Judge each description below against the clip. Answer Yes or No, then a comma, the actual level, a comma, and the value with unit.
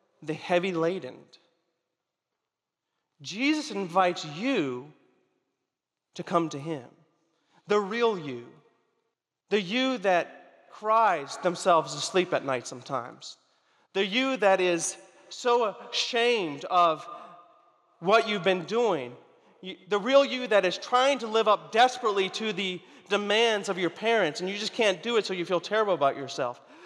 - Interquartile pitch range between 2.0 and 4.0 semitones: No, average, 4.4 semitones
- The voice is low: No, high, 190 Hz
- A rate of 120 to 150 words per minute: Yes, slow, 135 wpm